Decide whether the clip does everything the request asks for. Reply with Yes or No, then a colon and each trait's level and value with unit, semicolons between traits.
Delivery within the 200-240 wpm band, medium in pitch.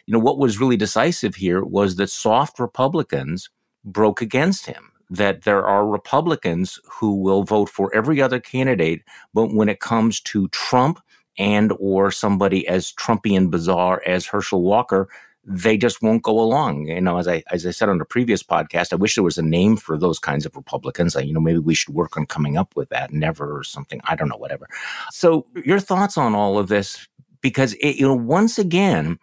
No: fast, 205 wpm; low, 105 Hz